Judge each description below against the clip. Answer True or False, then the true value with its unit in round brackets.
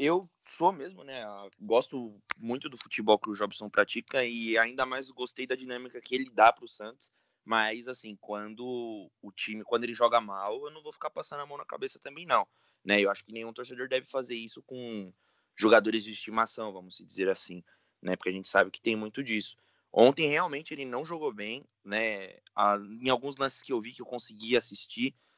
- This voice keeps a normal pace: False (205 wpm)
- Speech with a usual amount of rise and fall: True (3.4 semitones)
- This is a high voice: False (120 Hz)